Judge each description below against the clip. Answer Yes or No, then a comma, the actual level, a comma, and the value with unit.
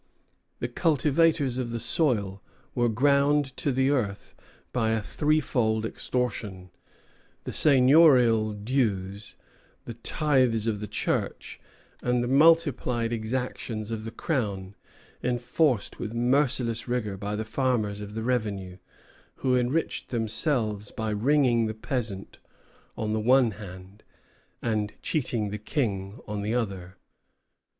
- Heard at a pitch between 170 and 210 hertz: No, low, 115 Hz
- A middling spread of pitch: Yes, average, 3.6 semitones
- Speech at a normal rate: No, slow, 125 wpm